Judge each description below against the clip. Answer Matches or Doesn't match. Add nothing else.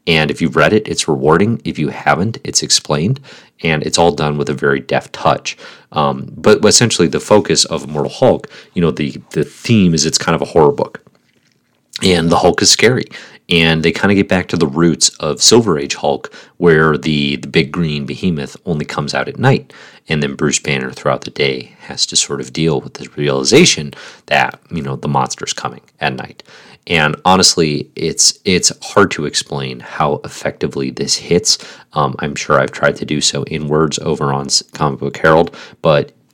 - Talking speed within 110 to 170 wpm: Doesn't match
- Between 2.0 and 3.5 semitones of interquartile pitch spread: Matches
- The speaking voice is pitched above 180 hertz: Doesn't match